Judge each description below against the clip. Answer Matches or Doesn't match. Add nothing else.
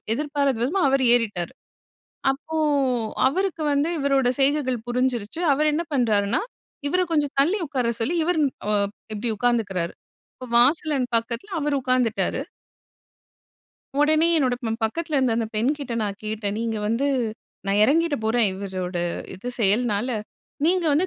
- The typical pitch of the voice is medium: Doesn't match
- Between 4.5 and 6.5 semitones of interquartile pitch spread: Matches